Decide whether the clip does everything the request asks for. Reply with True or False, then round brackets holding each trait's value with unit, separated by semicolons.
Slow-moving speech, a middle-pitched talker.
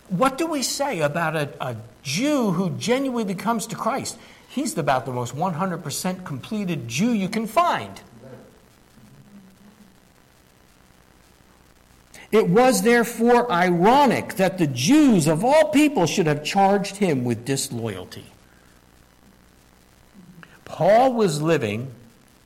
True (110 wpm; 175 Hz)